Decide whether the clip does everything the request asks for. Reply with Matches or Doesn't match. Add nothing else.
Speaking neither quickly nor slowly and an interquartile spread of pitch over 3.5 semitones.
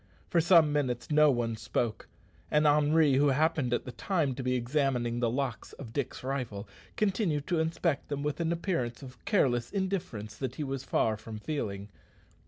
Matches